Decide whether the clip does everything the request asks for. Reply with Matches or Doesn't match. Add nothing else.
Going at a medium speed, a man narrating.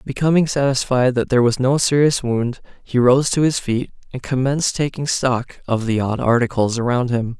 Matches